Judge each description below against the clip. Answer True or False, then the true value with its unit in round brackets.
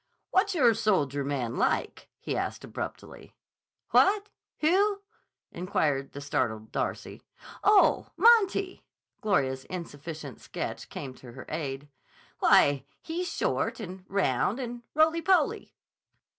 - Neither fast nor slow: False (115 wpm)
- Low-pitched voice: False (185 Hz)